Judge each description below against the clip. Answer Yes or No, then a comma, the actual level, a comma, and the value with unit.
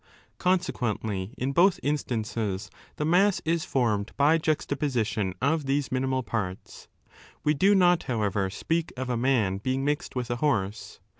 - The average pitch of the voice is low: Yes, low, 130 Hz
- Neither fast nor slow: Yes, average, 150 wpm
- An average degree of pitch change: No, wide, 5.8 semitones